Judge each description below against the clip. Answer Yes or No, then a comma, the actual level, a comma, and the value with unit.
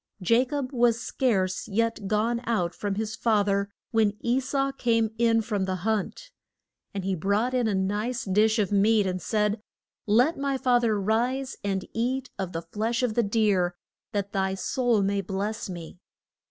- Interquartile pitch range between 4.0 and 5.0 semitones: No, average, 3.3 semitones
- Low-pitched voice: No, high, 215 Hz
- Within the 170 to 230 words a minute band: Yes, average, 180 wpm